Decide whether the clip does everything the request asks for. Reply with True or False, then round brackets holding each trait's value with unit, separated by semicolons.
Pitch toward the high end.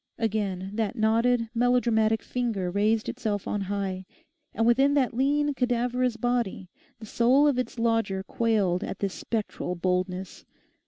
True (225 Hz)